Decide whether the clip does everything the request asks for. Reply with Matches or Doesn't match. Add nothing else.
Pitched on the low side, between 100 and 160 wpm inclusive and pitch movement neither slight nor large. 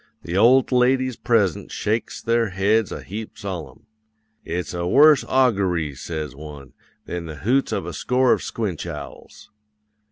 Doesn't match